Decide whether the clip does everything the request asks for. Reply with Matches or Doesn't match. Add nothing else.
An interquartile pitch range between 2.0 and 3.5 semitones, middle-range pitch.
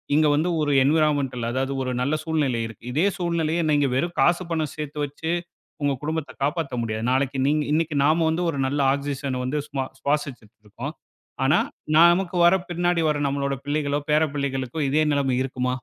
Matches